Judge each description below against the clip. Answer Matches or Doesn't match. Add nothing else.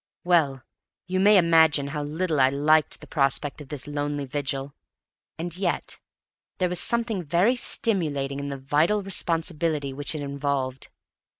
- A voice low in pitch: Doesn't match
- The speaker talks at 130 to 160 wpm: Matches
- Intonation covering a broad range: Doesn't match